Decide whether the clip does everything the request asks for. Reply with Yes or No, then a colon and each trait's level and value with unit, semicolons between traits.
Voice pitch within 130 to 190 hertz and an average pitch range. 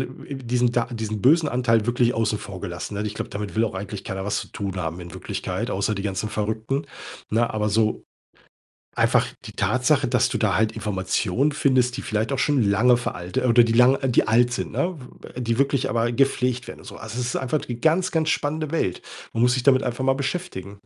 No: low, 120 Hz; average, 3.8 semitones